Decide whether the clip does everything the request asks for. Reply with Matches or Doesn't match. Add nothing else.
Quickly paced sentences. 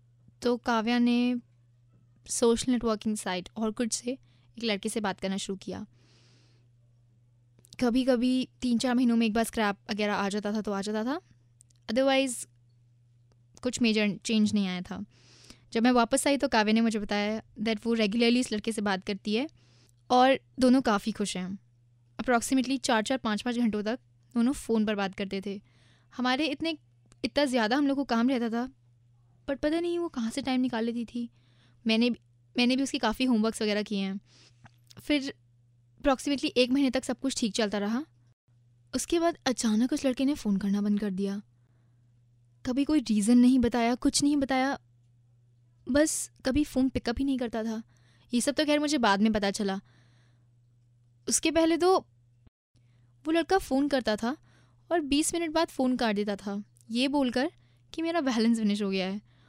Doesn't match